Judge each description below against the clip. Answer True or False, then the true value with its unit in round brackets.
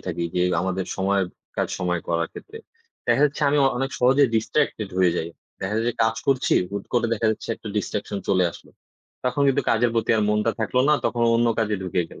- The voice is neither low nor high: False (110 Hz)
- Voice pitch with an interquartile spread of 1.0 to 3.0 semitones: False (4.6 semitones)